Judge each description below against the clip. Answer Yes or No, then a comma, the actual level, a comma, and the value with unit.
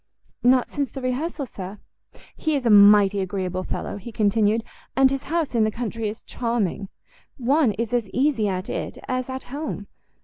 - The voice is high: Yes, high, 230 Hz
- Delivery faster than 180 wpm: No, average, 175 wpm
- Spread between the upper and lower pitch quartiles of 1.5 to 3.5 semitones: No, average, 4.3 semitones